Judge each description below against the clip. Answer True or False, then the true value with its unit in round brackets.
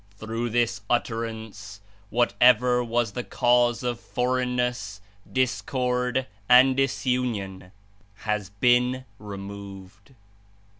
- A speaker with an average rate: False (90 wpm)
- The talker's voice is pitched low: True (120 Hz)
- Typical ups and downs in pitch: True (3.1 semitones)